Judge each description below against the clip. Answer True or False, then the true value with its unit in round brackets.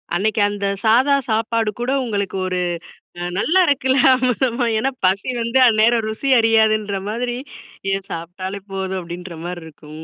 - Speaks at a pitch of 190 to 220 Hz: True (215 Hz)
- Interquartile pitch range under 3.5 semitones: False (3.8 semitones)